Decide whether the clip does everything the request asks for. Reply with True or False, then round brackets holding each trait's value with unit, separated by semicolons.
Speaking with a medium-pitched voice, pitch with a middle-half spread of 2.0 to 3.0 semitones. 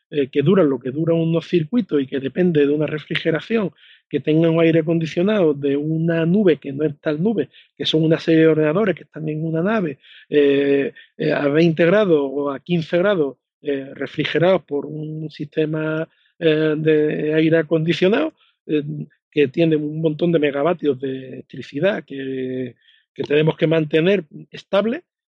True (155 Hz; 2.4 semitones)